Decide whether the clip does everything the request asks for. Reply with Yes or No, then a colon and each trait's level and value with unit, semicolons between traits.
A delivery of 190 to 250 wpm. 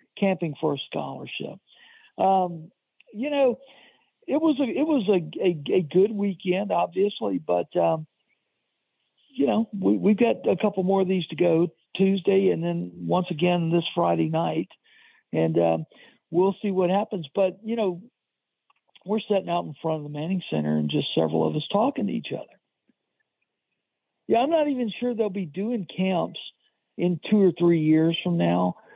No: average, 170 wpm